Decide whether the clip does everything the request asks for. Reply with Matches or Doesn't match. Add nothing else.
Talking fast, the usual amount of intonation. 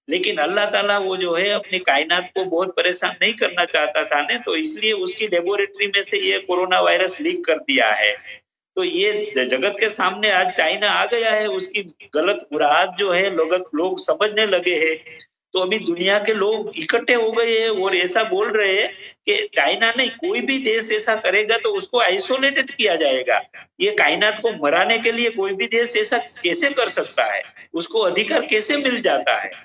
Doesn't match